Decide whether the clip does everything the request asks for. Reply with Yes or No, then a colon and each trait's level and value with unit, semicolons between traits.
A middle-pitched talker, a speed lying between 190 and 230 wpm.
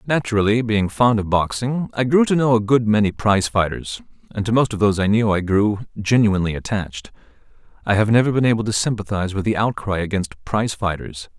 No: low, 105 Hz; average, 200 wpm